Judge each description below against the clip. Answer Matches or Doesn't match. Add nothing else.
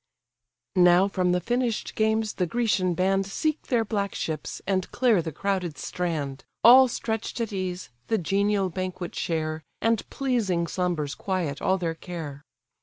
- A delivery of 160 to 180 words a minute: Doesn't match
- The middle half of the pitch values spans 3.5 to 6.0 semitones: Matches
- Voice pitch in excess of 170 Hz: Matches